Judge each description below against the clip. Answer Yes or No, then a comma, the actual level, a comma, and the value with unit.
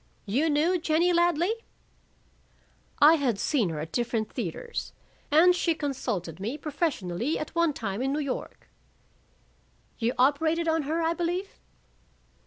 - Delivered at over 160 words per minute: No, slow, 135 wpm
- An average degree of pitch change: No, wide, 5.8 semitones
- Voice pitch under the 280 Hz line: No, very high, 300 Hz